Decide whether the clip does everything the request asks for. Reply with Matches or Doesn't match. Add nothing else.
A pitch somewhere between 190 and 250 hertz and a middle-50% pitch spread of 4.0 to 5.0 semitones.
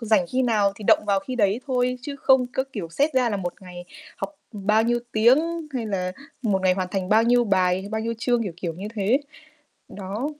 Matches